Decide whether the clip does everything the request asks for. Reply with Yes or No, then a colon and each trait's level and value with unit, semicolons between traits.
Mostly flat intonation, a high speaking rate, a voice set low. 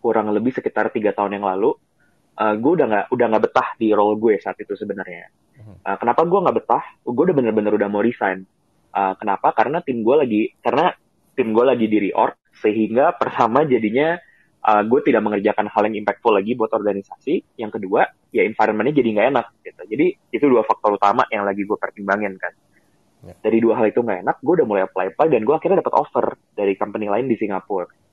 Yes: narrow, 2.0 semitones; fast, 200 wpm; low, 105 Hz